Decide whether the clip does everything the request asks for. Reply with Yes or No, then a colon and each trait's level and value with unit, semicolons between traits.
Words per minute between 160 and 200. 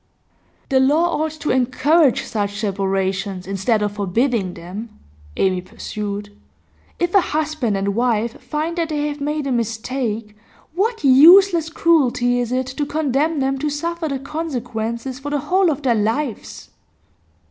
No: average, 145 wpm